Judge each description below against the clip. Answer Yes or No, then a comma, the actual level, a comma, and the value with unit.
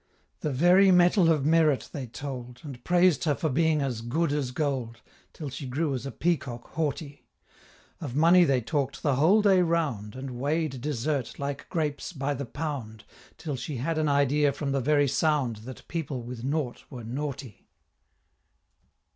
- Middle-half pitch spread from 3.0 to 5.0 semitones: Yes, average, 3.6 semitones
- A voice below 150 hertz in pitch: Yes, medium, 140 Hz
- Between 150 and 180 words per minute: Yes, average, 170 wpm